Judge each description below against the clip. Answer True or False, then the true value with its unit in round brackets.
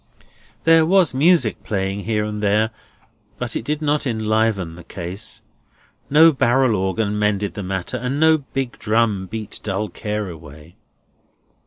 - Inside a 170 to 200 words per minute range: False (145 wpm)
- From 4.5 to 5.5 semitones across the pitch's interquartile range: True (5.2 semitones)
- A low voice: True (110 Hz)